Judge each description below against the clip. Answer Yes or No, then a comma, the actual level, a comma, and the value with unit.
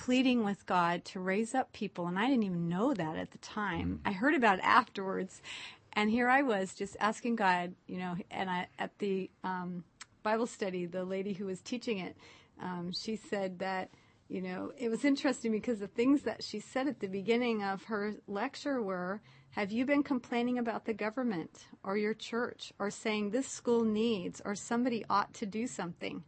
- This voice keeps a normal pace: Yes, average, 195 wpm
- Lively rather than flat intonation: No, average, 4.1 semitones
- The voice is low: No, high, 210 Hz